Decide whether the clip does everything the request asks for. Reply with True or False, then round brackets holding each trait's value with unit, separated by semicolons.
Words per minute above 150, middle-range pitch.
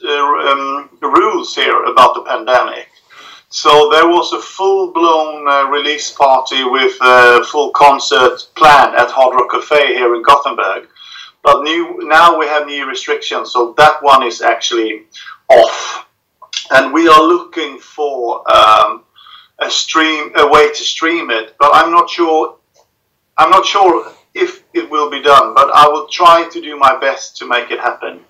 True (165 wpm; 150 Hz)